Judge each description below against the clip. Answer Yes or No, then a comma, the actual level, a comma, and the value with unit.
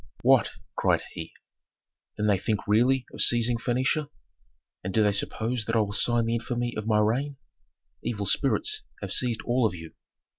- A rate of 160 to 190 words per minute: Yes, average, 175 wpm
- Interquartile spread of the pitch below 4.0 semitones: Yes, narrow, 2.5 semitones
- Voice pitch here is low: Yes, low, 115 Hz